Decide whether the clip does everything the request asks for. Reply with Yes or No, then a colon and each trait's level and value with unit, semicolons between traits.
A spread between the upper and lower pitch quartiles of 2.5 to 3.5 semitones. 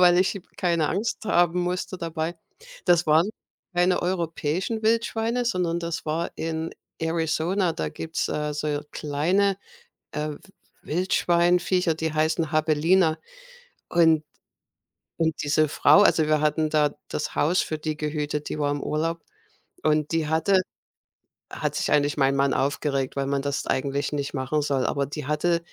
Yes: average, 2.8 semitones